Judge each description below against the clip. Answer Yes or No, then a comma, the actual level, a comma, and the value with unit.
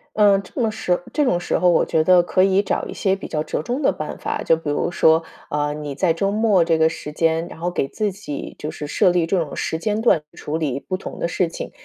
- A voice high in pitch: No, medium, 175 Hz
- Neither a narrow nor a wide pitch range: Yes, average, 3.5 semitones